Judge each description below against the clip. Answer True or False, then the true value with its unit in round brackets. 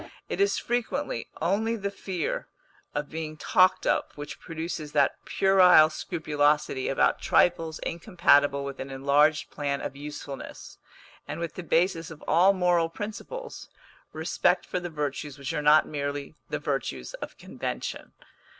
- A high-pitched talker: False (160 Hz)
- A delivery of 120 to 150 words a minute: True (140 wpm)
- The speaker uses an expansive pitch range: False (3.8 semitones)